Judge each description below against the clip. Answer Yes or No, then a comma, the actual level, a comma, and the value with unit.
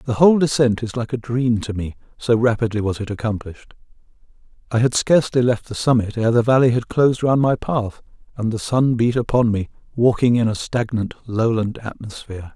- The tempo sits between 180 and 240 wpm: Yes, average, 190 wpm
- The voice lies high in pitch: No, low, 115 Hz